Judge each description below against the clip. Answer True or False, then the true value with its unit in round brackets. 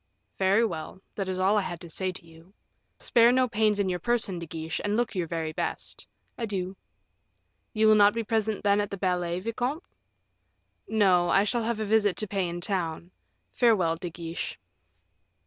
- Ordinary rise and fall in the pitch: True (3.8 semitones)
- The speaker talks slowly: False (185 wpm)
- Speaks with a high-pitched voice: True (195 Hz)